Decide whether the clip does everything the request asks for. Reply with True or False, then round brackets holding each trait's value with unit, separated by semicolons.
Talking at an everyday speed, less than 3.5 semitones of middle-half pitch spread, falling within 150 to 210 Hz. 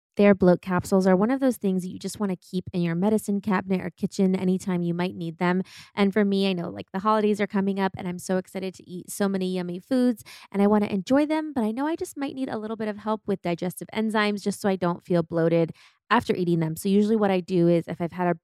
False (280 wpm; 2.9 semitones; 190 Hz)